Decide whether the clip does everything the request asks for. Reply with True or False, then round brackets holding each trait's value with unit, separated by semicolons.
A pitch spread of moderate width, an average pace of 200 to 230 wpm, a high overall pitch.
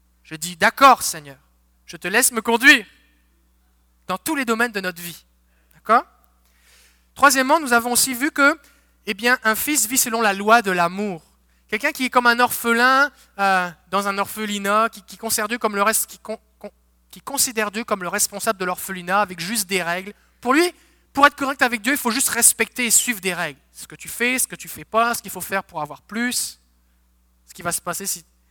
False (6.0 semitones; 210 wpm; 205 Hz)